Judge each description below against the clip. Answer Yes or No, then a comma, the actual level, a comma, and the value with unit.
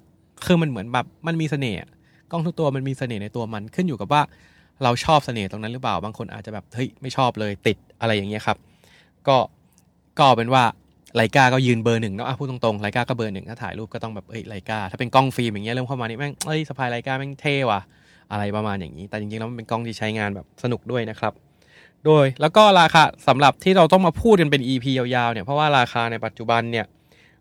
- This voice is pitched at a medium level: No, low, 120 Hz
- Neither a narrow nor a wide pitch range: Yes, average, 4.3 semitones